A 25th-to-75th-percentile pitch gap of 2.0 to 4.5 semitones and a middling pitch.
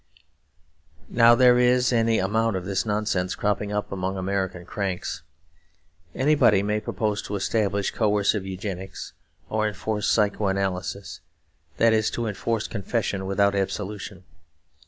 No: narrow, 2.4 semitones; low, 105 Hz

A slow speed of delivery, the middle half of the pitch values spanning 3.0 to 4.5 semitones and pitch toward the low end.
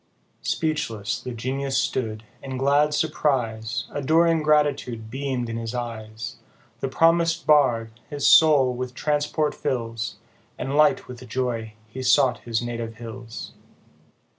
Yes: slow, 125 wpm; average, 4.2 semitones; low, 130 Hz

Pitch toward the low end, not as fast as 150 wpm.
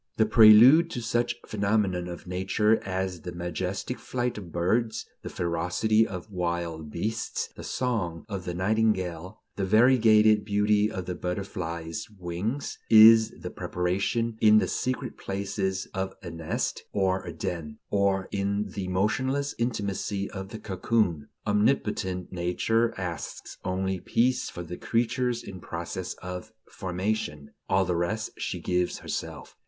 Yes: very low, 95 Hz; average, 140 wpm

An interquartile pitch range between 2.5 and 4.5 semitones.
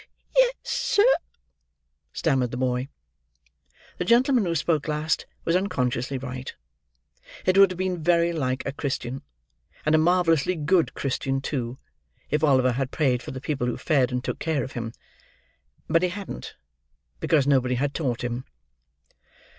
No: average, 5.0 semitones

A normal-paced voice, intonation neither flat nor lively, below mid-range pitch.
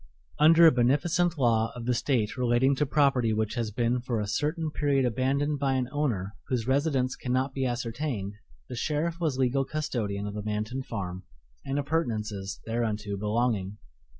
Yes: average, 165 wpm; average, 4.5 semitones; low, 125 Hz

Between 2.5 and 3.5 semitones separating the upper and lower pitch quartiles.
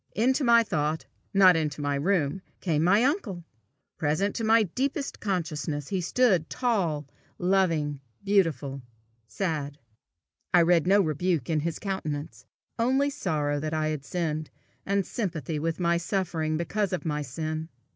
No: average, 4.6 semitones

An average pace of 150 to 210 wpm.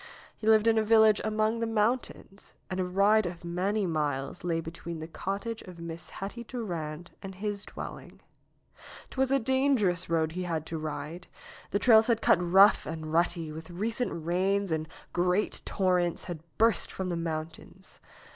Yes: average, 165 wpm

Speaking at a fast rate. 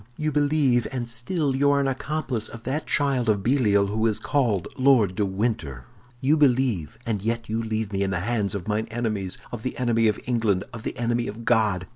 Yes: fast, 210 wpm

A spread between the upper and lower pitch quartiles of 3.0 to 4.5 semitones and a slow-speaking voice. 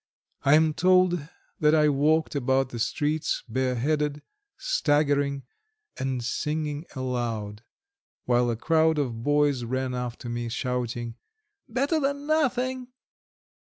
Yes: average, 4.2 semitones; slow, 115 wpm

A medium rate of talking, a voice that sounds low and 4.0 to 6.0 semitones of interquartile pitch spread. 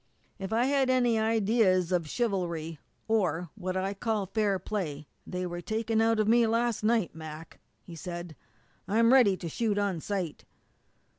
No: average, 160 wpm; high, 200 Hz; average, 4.4 semitones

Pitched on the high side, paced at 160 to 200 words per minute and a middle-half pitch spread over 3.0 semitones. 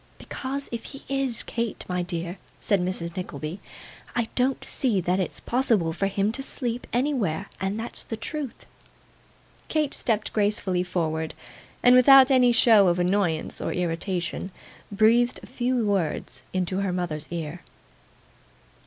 No: high, 200 Hz; average, 145 wpm; wide, 5.5 semitones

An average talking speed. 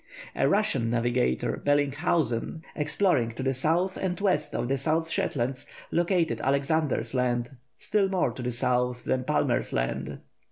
Yes: average, 145 wpm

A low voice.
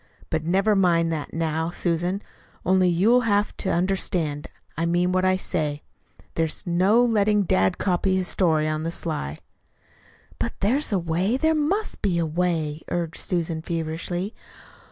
No: medium, 175 Hz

